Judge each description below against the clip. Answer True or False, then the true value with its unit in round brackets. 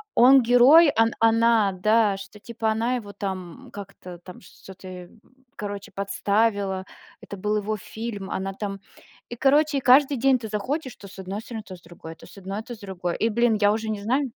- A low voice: False (210 Hz)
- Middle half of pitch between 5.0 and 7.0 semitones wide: False (3.3 semitones)